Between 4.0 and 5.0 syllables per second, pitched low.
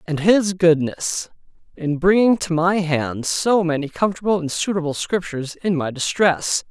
No: 4.7 syllables/s; medium, 170 Hz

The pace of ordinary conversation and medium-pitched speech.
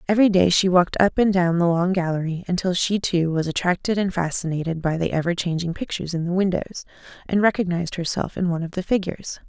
No: fast, 210 wpm; medium, 180 Hz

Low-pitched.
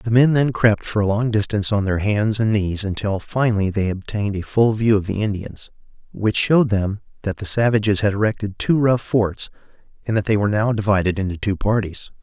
Yes: low, 105 Hz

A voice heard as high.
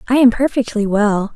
Yes: high, 230 Hz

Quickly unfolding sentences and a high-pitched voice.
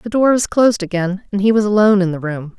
Yes: fast, 280 wpm; high, 200 Hz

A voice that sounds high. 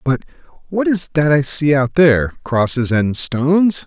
No: medium, 145 Hz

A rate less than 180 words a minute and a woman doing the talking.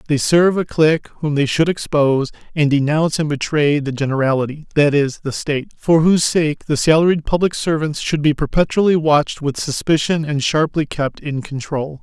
No: average, 170 wpm; male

